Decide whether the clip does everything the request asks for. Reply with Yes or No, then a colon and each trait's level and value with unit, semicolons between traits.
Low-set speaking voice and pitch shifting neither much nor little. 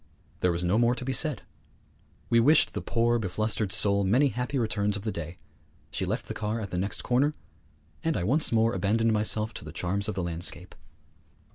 Yes: low, 110 Hz; average, 3.3 semitones